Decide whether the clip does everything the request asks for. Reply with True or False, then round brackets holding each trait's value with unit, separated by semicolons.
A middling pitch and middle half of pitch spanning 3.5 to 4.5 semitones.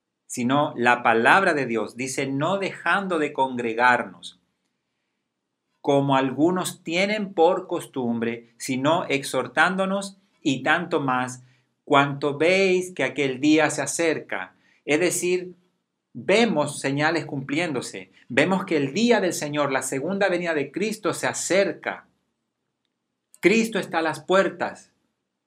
False (150 Hz; 5.3 semitones)